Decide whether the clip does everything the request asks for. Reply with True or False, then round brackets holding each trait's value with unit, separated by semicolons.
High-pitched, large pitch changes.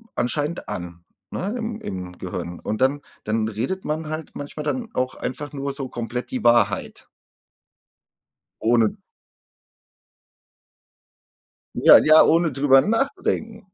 False (140 Hz; 7.0 semitones)